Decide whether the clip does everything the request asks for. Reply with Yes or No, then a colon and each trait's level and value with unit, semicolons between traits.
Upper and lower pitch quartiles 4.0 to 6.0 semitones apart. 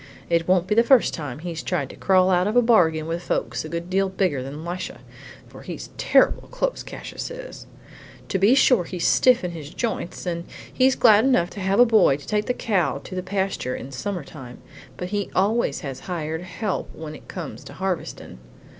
Yes: average, 4.6 semitones